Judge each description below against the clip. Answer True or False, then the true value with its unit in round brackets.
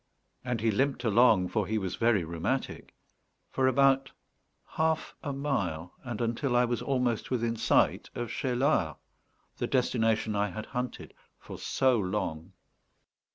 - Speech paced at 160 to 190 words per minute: False (140 wpm)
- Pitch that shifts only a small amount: False (4.1 semitones)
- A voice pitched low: True (120 Hz)